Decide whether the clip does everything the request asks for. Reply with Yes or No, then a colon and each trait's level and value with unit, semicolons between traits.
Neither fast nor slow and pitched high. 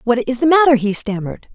No: fast, 235 wpm; very high, 250 Hz